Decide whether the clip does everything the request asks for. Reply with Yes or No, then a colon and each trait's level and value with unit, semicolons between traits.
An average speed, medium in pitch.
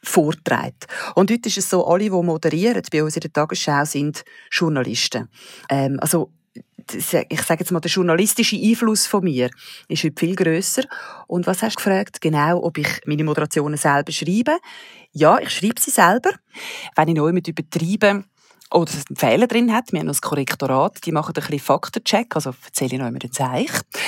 Yes: average, 170 wpm; medium, 170 Hz